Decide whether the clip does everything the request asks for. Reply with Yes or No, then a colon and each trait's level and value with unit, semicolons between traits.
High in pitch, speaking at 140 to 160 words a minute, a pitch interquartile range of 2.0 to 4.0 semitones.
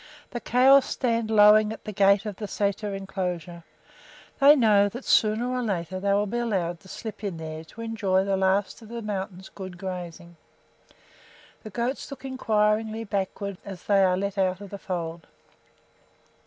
No: high, 200 Hz; average, 170 wpm; average, 2.9 semitones